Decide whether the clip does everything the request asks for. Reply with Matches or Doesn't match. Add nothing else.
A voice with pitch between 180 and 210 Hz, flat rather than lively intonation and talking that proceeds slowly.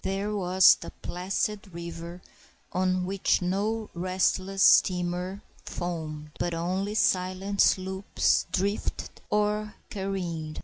Matches